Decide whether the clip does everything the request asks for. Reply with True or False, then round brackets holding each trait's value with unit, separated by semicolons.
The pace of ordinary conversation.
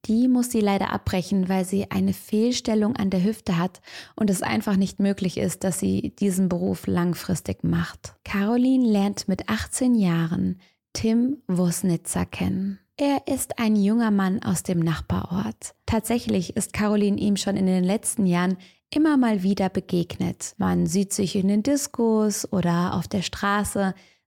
True (160 wpm)